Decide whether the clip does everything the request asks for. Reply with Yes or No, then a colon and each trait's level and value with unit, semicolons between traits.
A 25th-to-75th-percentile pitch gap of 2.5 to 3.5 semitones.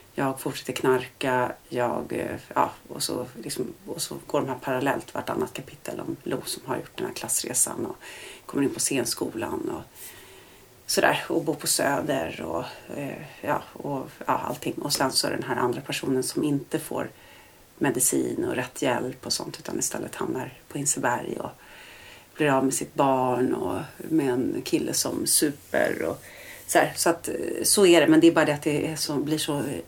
Yes: average, 3.2 semitones